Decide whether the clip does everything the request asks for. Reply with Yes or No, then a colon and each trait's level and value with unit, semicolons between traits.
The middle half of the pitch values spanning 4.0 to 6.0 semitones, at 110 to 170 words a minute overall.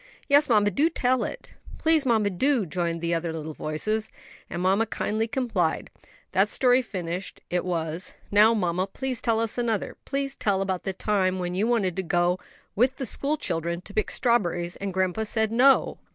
No: average, 5.3 semitones; average, 180 wpm